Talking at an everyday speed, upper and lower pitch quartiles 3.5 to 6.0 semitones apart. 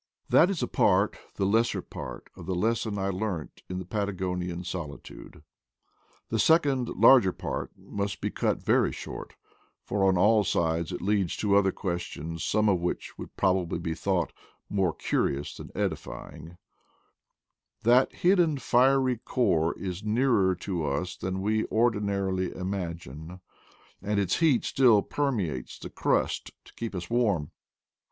Yes: average, 150 wpm; average, 4.2 semitones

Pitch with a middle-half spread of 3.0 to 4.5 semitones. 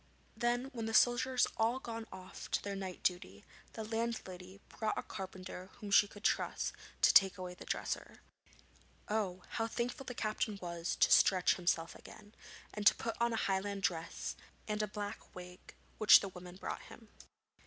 Yes: average, 3.5 semitones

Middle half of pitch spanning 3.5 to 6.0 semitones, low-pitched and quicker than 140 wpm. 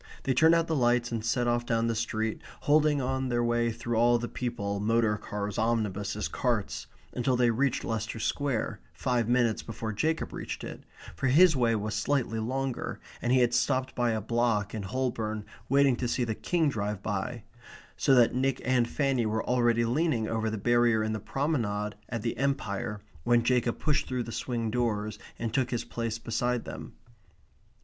No: narrow, 2.5 semitones; low, 120 Hz; average, 190 wpm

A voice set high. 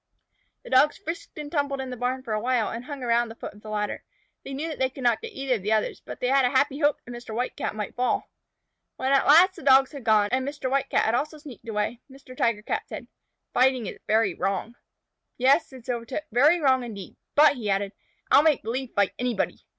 Yes: very high, 255 Hz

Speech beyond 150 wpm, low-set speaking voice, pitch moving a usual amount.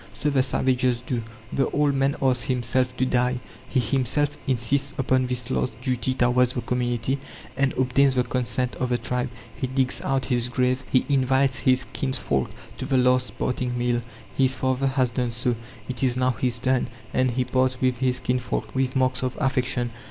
No: average, 185 wpm; low, 130 Hz; narrow, 1.0 semitones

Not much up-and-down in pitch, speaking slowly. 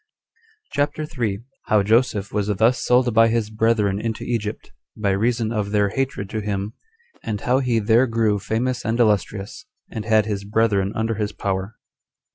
No: narrow, 2.2 semitones; average, 165 wpm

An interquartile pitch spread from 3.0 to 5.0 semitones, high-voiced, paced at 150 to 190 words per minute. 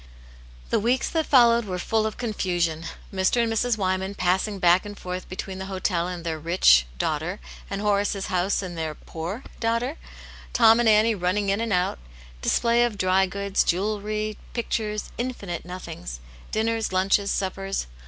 Yes: average, 3.4 semitones; high, 200 Hz; average, 170 wpm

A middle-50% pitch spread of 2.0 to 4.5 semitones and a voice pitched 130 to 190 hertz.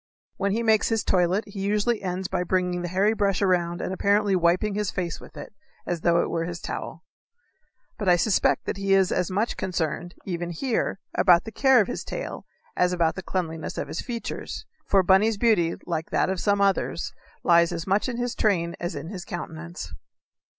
Yes: average, 2.9 semitones; medium, 185 Hz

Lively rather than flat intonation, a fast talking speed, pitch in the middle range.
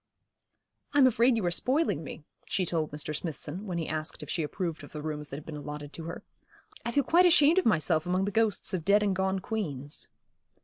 Yes: wide, 6.3 semitones; fast, 220 wpm; medium, 180 Hz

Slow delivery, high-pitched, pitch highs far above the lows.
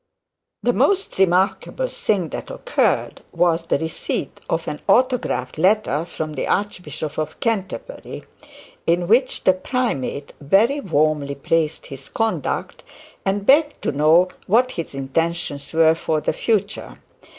No: slow, 130 wpm; medium, 170 Hz; wide, 5.8 semitones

